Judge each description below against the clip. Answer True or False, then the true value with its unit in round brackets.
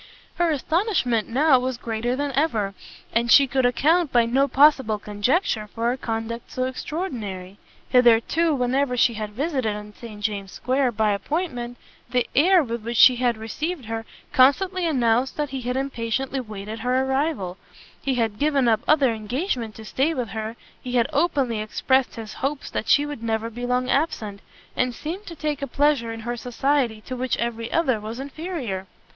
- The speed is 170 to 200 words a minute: True (175 wpm)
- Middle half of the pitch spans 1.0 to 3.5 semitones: False (4.0 semitones)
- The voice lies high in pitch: True (250 Hz)